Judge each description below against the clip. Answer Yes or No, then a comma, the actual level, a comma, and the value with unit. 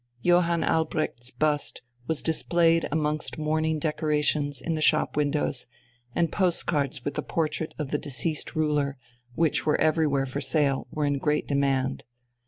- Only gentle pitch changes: Yes, narrow, 1.9 semitones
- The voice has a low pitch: No, medium, 150 Hz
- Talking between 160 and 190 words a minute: No, average, 145 wpm